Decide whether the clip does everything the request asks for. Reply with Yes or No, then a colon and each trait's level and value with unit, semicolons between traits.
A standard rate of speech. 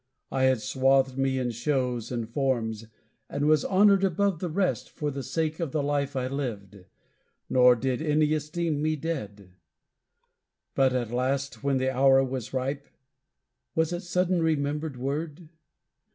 Yes: average, 150 wpm